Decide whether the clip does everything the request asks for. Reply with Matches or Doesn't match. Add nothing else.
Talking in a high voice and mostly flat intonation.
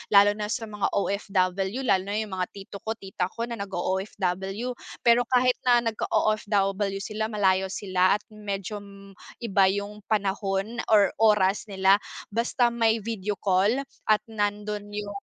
Matches